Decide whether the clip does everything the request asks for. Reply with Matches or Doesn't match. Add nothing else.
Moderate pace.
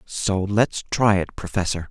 Matches